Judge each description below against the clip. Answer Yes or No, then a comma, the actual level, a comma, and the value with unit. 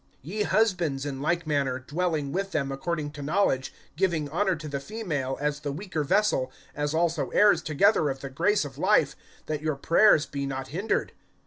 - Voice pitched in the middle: Yes, medium, 155 Hz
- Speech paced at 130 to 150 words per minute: No, average, 185 wpm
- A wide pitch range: No, average, 4.5 semitones